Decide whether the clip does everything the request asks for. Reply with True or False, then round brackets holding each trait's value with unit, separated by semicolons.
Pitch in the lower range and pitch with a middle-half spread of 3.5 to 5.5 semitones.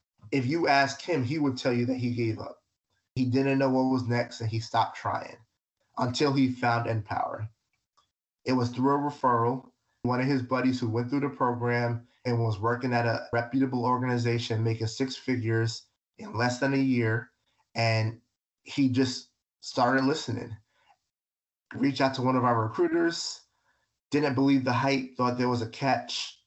False (125 Hz; 2.4 semitones)